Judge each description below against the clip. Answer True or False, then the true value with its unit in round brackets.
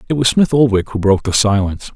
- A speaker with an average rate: False (245 wpm)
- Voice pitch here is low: True (115 Hz)